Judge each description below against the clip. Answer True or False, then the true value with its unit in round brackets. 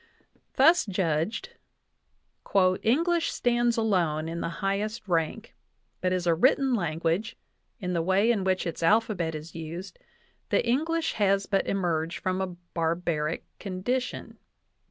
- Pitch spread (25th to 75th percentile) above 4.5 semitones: True (5.2 semitones)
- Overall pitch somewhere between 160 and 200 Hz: True (190 Hz)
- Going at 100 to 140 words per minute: True (135 wpm)